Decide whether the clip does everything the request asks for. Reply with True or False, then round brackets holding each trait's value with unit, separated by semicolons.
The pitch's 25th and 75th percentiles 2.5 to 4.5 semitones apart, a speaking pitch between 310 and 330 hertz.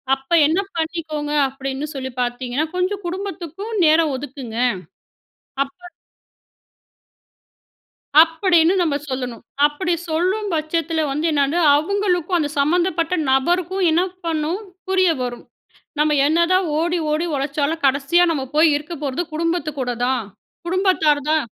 True (3.8 semitones; 315 Hz)